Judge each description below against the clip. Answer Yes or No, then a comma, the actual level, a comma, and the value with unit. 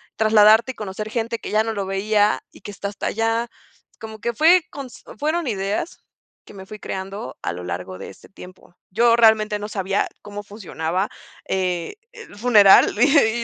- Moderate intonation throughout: Yes, average, 3.0 semitones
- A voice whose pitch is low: No, high, 210 Hz